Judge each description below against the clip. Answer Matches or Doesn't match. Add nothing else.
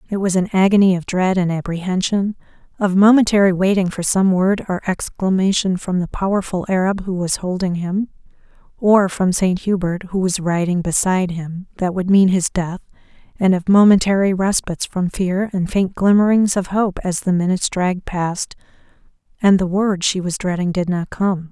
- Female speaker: Matches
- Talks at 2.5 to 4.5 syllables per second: Doesn't match